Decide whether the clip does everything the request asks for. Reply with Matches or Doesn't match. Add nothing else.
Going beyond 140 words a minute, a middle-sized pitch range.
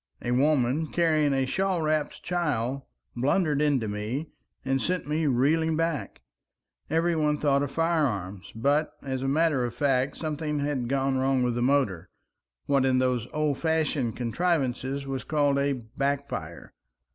Matches